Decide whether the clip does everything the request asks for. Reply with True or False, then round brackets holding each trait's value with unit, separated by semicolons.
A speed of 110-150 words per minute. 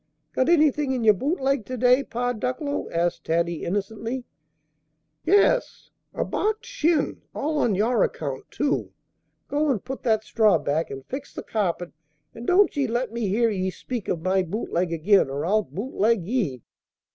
False (175 wpm)